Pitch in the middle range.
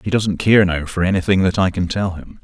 No: very low, 95 Hz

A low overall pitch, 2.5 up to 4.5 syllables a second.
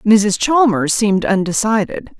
No: high, 210 Hz; 4.2 syllables/s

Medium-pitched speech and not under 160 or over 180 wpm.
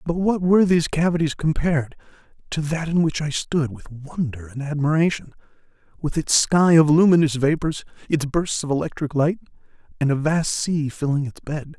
Yes: medium, 155 Hz; average, 175 wpm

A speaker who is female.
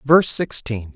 No: male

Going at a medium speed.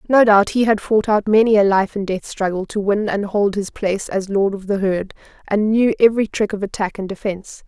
No: fast, 240 wpm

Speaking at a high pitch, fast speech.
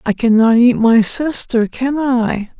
No: high, 240 Hz; average, 160 wpm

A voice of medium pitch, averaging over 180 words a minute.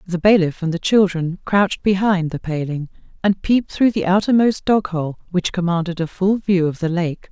Yes: medium, 180 Hz; average, 195 wpm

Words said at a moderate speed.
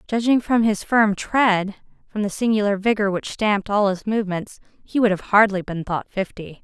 Yes: average, 190 wpm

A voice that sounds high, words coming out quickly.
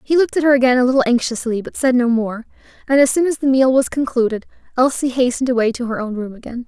Yes: very high, 250 Hz; fast, 250 wpm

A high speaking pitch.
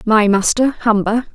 Yes: high, 220 Hz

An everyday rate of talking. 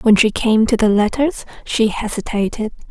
Yes: average, 165 wpm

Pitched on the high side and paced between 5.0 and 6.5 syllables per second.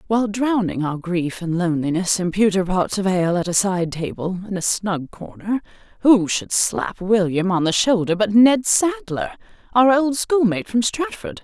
No: high, 200 Hz; 4.8 syllables/s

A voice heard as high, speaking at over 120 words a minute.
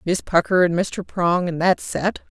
No: medium, 175 Hz; average, 200 wpm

